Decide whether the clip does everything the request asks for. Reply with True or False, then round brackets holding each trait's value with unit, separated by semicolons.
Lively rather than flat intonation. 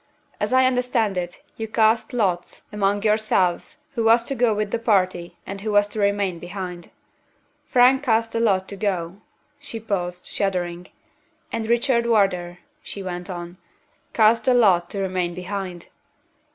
False (3.9 semitones)